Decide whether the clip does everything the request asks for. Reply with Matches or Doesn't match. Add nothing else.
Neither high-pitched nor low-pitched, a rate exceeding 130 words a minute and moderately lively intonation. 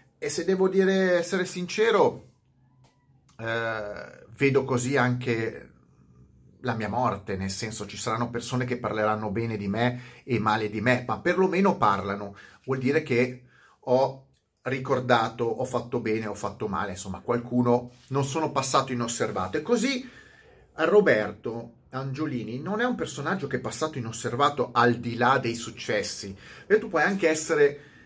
Doesn't match